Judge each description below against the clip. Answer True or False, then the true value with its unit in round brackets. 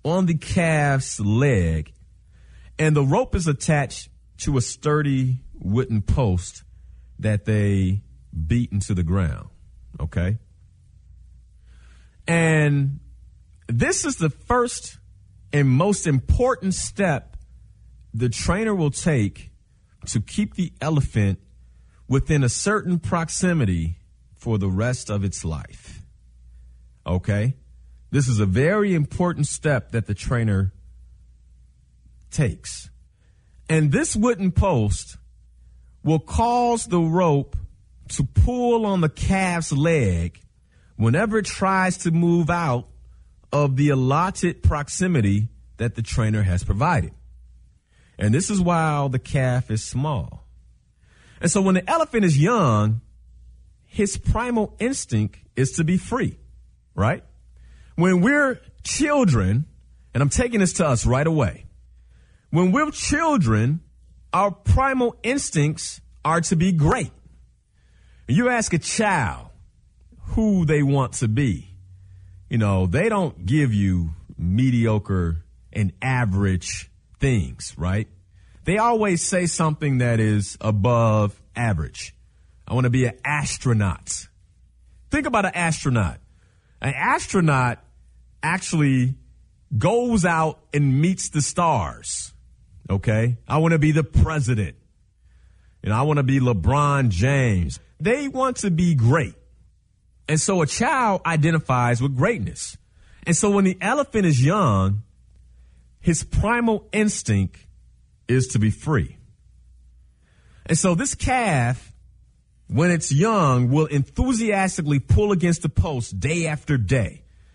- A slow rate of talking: True (120 wpm)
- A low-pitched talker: True (120 Hz)